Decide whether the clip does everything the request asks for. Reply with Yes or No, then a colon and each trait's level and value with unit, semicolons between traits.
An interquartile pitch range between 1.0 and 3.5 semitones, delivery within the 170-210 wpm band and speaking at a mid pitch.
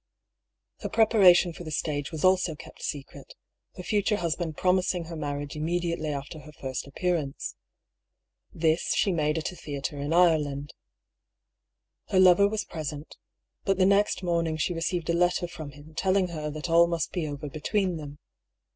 Yes: average, 3.1 semitones; average, 175 wpm; medium, 165 Hz